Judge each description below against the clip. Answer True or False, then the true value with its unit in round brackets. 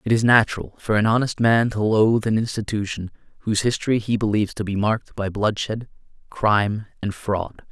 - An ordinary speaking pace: True (180 wpm)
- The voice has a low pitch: True (110 Hz)